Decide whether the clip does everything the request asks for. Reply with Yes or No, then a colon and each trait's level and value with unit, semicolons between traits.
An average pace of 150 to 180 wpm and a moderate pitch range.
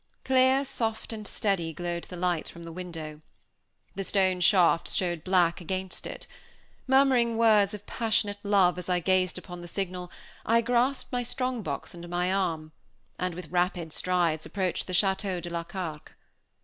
Yes: average, 165 wpm; average, 3.4 semitones